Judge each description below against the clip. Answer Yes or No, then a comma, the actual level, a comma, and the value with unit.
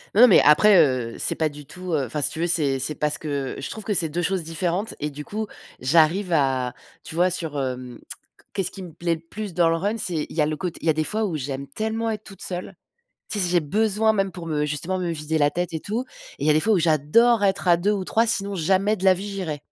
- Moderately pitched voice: Yes, medium, 170 Hz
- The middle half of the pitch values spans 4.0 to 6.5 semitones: Yes, average, 4.7 semitones